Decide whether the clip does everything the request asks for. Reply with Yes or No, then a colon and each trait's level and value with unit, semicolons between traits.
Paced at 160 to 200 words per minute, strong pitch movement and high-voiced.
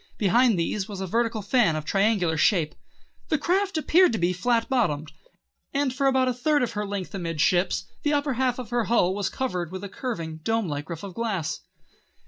Yes: average, 195 wpm; wide, 6.2 semitones; high, 210 Hz